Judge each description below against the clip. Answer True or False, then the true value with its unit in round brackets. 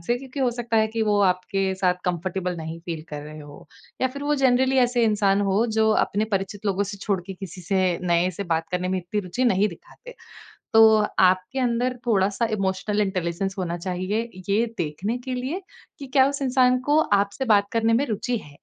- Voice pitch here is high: True (205 Hz)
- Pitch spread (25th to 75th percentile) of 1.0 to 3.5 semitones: False (4.8 semitones)